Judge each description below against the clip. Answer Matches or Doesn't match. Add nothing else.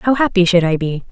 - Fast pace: Matches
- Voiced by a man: Doesn't match